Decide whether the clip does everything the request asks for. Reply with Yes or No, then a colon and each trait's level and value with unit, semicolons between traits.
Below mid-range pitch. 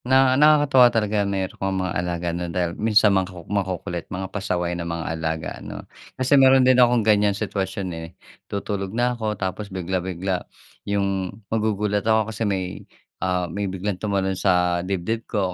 Yes: very low, 95 Hz